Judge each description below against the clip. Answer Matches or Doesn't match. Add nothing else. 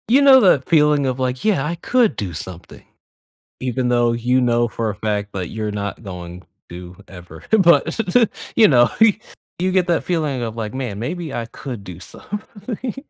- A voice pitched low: Matches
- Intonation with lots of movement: Matches